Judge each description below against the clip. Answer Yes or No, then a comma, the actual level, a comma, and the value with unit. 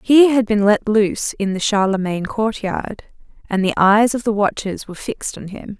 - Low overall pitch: No, high, 210 Hz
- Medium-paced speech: Yes, average, 195 wpm